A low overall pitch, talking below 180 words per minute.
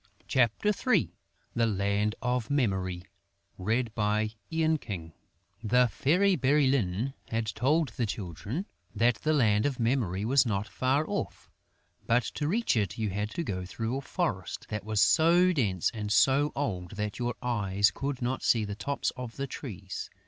Yes: low, 115 Hz; average, 150 wpm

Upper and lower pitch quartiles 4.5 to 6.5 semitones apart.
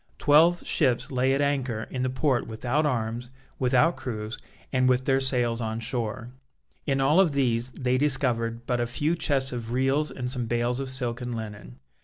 No: narrow, 2.4 semitones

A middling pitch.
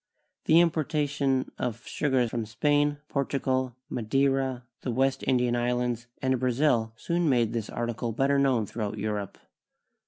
No: low, 130 Hz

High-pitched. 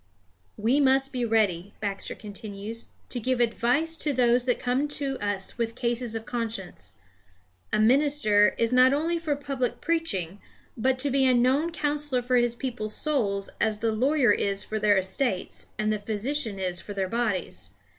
Yes: high, 240 Hz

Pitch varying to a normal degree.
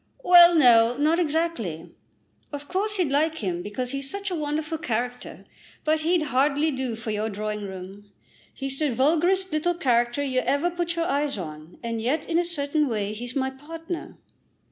No: wide, 5.8 semitones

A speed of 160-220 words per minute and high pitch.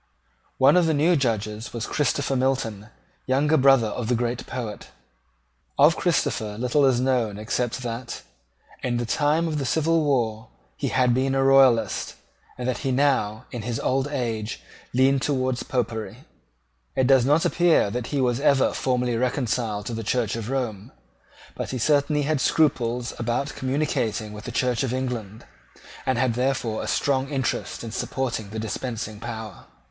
No: average, 165 wpm; low, 125 Hz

